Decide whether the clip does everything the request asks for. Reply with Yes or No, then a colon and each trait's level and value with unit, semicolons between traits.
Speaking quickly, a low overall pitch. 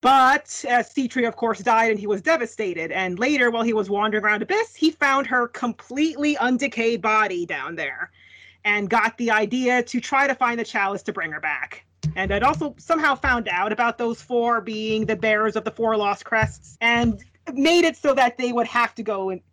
No: fast, 210 wpm; high, 230 Hz